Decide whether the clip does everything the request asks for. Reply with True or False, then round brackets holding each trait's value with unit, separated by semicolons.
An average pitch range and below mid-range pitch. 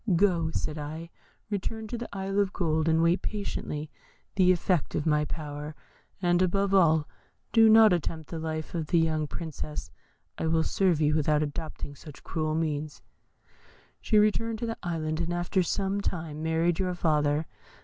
False (3.5 semitones; 165 Hz)